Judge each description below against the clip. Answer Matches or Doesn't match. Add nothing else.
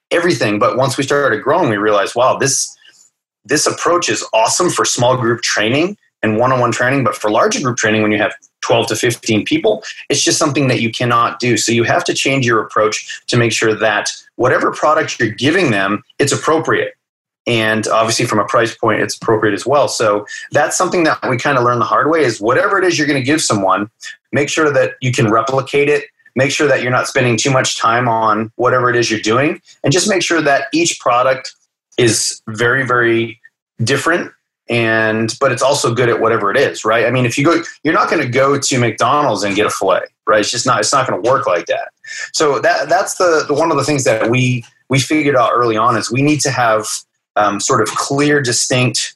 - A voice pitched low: Matches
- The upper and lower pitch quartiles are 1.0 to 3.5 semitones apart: Doesn't match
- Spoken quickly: Matches